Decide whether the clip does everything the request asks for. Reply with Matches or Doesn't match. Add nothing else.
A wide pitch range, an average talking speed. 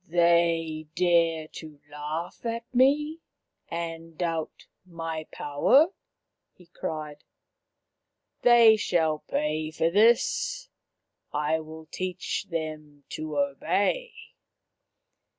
Doesn't match